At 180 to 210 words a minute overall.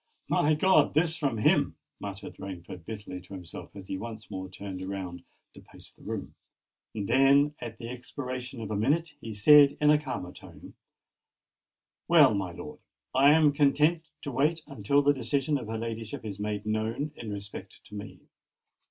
No: average, 170 wpm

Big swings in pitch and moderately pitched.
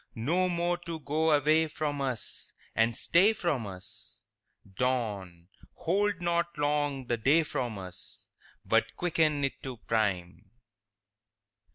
Yes: wide, 6.7 semitones; medium, 145 Hz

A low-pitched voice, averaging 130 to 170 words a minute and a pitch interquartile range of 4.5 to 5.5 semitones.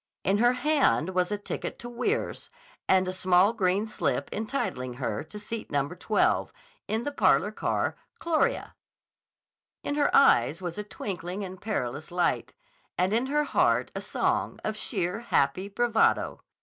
No: high, 205 Hz; average, 155 wpm; average, 5.0 semitones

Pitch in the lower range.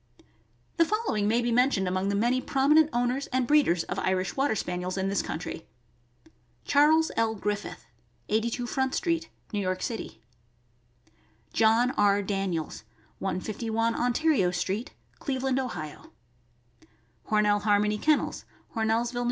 No: high, 225 Hz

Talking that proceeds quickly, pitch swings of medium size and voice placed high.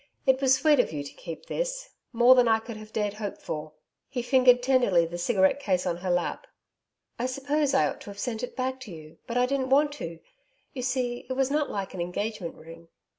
No: fast, 225 wpm; wide, 5.9 semitones; high, 240 Hz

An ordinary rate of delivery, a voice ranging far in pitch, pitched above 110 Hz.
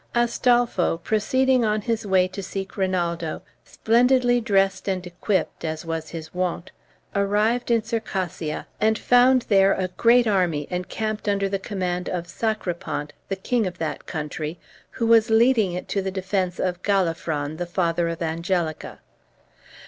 No: average, 150 wpm; average, 4.1 semitones; high, 190 Hz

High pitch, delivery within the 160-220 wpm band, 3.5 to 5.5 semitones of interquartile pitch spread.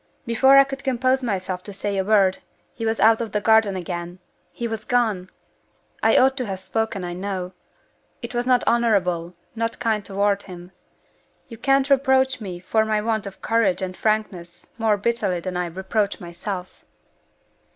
Yes: high, 210 Hz; average, 170 wpm; average, 3.9 semitones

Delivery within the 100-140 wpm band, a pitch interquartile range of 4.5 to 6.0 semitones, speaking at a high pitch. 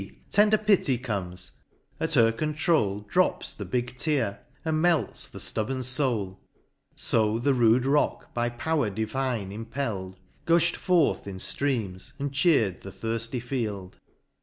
No: slow, 135 wpm; average, 5.2 semitones; low, 120 Hz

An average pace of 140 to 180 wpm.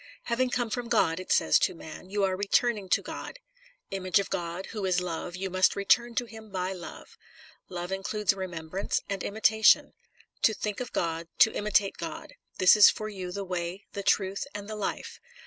No: average, 195 wpm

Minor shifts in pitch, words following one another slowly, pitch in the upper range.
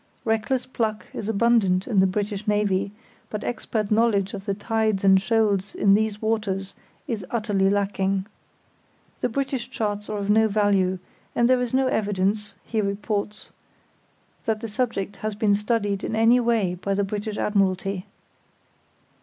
No: narrow, 2.1 semitones; average, 155 wpm; high, 210 Hz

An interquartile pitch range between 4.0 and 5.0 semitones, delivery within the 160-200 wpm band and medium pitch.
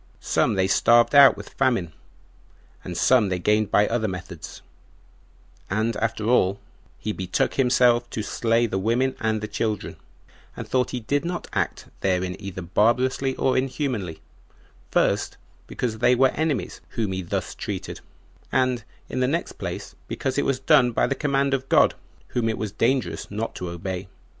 No: average, 4.7 semitones; average, 165 wpm; low, 115 Hz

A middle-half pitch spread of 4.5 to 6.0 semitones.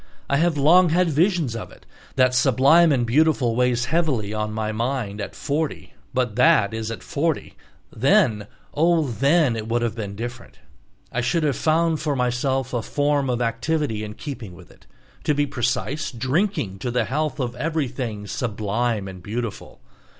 Yes: average, 4.9 semitones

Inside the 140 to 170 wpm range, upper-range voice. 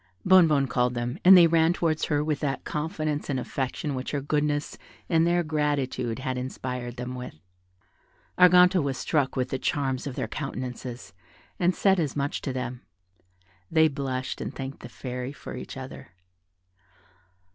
No: average, 160 wpm; medium, 140 Hz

